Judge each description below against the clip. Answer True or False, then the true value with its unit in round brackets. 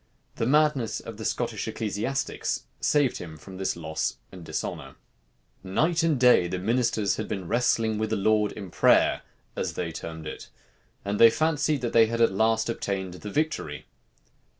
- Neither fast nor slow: True (170 wpm)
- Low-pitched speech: True (110 Hz)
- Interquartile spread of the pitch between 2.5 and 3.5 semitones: False (4.9 semitones)